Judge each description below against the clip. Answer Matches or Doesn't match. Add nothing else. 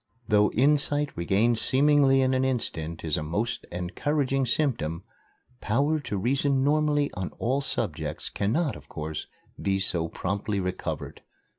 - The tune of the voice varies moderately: Doesn't match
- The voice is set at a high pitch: Doesn't match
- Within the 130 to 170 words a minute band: Matches